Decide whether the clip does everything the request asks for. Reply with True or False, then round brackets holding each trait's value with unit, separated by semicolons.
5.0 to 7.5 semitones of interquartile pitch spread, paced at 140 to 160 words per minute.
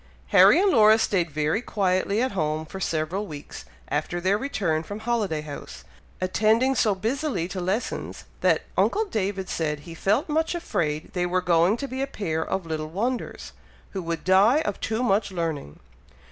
False (5.3 semitones; 175 wpm)